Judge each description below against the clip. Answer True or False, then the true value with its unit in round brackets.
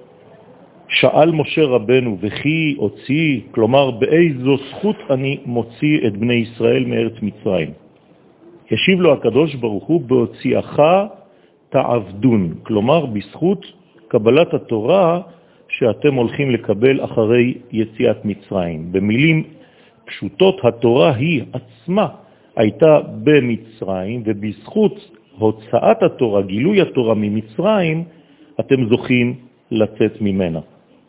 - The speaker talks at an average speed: False (90 wpm)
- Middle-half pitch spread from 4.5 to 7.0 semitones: True (5.3 semitones)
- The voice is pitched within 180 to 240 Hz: False (125 Hz)